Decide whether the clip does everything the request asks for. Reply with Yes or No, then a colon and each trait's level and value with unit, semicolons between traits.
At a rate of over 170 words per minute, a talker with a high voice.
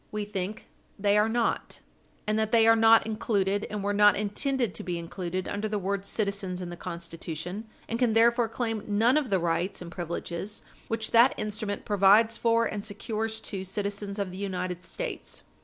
Yes: average, 185 wpm; high, 205 Hz